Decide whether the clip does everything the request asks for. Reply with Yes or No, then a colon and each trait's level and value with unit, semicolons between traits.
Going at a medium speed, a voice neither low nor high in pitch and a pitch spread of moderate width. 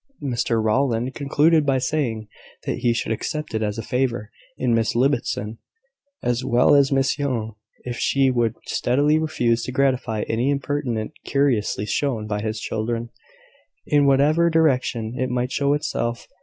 No: average, 155 wpm; low, 125 Hz; average, 3.7 semitones